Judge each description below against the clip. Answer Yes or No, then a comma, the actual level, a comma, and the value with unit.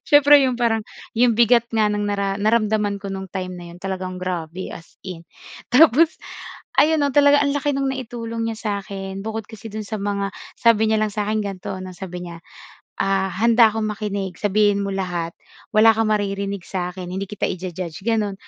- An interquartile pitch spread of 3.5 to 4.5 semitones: No, average, 3.0 semitones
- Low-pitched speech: No, high, 205 Hz